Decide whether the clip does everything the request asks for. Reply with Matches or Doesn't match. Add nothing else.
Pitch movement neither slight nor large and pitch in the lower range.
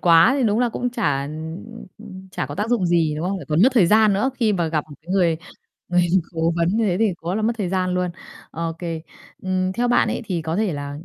Doesn't match